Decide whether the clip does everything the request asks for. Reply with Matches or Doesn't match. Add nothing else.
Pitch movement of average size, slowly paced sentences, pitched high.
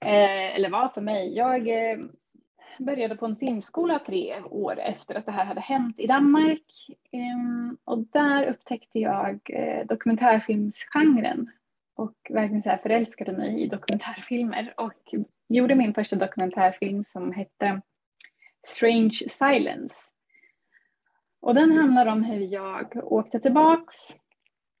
Matches